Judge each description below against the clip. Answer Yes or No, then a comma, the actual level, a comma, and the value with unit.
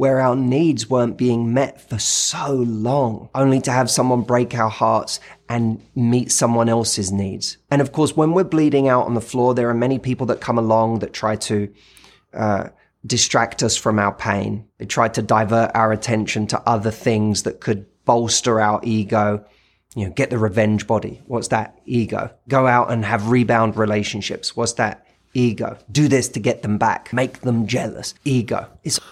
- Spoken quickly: No, average, 185 wpm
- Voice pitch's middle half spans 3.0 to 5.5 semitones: No, narrow, 2.5 semitones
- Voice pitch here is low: Yes, low, 115 Hz